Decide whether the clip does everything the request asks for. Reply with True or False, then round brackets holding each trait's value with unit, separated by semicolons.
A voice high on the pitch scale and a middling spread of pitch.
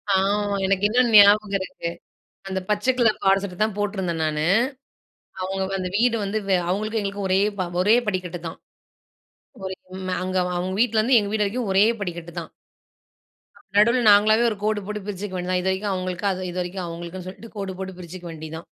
False (195 Hz; 2.3 semitones)